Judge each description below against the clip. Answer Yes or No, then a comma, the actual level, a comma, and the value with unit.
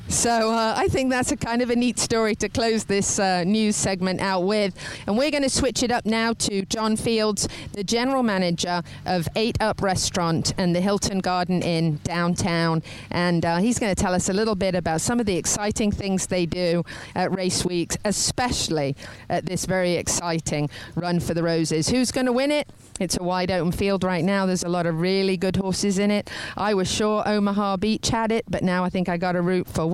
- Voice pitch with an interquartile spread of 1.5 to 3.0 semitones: No, average, 3.6 semitones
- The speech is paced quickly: Yes, fast, 220 wpm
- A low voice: No, high, 190 Hz